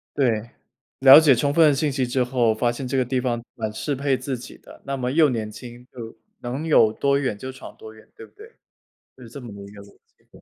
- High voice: No, low, 125 Hz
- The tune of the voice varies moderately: Yes, average, 3.0 semitones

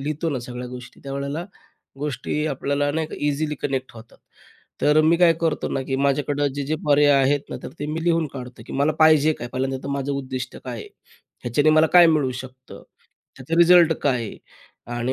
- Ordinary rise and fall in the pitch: Yes, average, 3.0 semitones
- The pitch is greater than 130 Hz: Yes, medium, 140 Hz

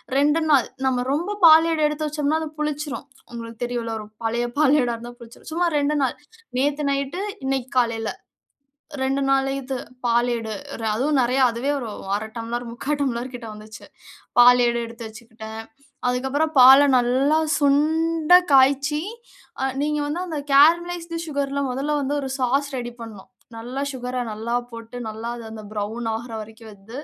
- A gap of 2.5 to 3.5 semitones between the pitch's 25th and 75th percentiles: No, average, 3.9 semitones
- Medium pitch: No, very high, 260 Hz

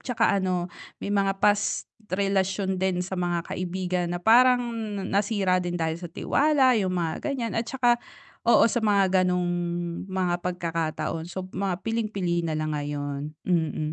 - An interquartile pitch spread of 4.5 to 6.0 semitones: No, average, 2.7 semitones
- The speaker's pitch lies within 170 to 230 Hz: Yes, medium, 185 Hz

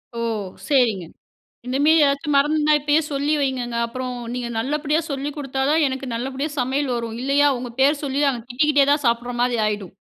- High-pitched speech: Yes, very high, 270 Hz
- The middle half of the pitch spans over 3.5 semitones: No, average, 2.9 semitones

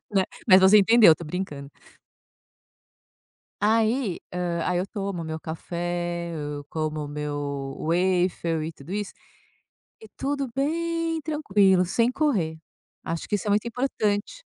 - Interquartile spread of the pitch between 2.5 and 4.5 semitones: No, wide, 5.5 semitones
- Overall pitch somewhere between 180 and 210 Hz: Yes, medium, 185 Hz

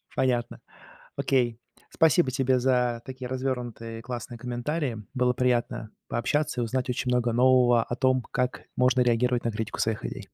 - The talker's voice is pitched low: Yes, low, 125 Hz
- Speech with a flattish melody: Yes, narrow, 1.5 semitones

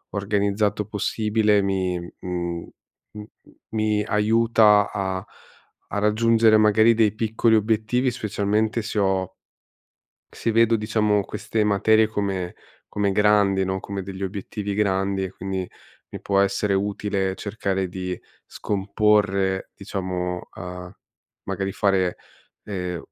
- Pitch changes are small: Yes, narrow, 1.9 semitones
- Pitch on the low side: Yes, low, 100 Hz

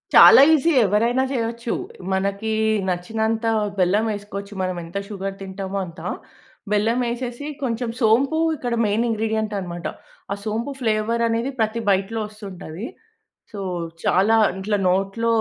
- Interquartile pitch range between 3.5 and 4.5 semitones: No, average, 2.9 semitones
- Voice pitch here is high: Yes, high, 215 Hz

